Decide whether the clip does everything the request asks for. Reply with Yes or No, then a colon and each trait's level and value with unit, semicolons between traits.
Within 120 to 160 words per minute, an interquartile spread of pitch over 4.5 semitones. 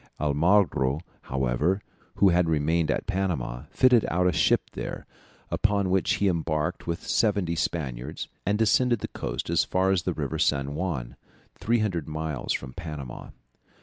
Yes: average, 150 wpm; average, 4.9 semitones